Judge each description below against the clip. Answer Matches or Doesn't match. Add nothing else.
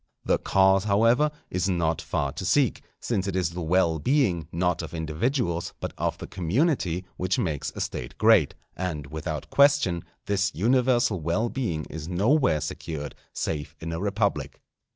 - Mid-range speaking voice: Doesn't match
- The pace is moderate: Matches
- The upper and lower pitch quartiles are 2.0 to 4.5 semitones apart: Doesn't match